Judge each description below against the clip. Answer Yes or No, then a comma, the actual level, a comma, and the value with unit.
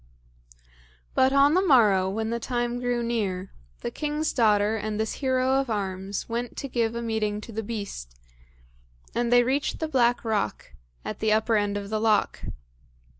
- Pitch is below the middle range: No, high, 225 Hz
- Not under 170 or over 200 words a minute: Yes, average, 175 wpm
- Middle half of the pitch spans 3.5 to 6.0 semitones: No, average, 3.1 semitones